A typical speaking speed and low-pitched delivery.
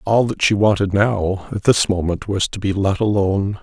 No: fast, 215 wpm; low, 100 Hz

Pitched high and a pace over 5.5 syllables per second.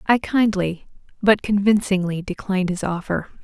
No: high, 195 Hz; 4.9 syllables/s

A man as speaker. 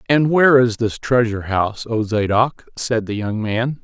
Yes: male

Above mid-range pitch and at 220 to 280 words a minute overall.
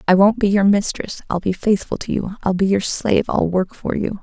Yes: high, 195 Hz; fast, 255 wpm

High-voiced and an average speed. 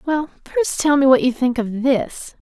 No: very high, 270 Hz; fast, 220 wpm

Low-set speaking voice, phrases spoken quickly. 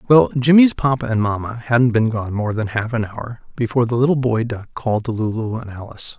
Yes: low, 115 Hz; fast, 225 wpm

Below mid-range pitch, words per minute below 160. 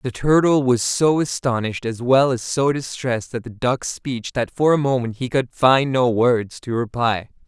No: low, 125 Hz; average, 200 wpm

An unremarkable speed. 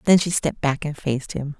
No: fast, 265 wpm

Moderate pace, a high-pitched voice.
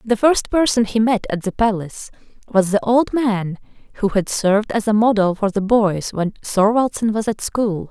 Yes: average, 195 wpm; high, 215 Hz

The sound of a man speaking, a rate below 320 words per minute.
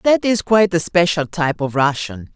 No: female; fast, 205 wpm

